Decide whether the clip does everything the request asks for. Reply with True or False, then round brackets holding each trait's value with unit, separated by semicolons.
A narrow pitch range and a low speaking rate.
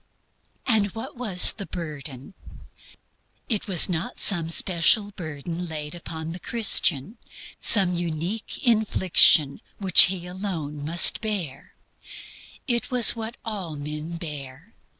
False (5.1 semitones; 115 wpm)